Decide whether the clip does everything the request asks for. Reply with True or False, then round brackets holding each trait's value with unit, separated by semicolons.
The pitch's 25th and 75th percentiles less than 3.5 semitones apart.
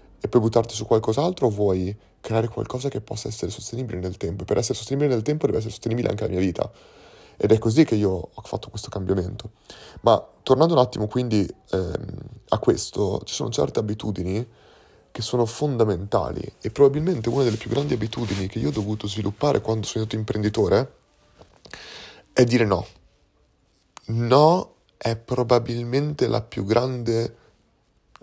True (2.9 semitones)